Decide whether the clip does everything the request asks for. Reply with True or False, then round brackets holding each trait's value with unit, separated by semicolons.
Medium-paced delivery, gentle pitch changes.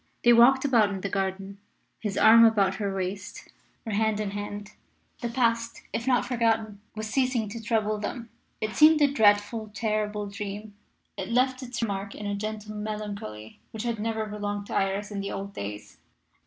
True (180 wpm; 2.3 semitones)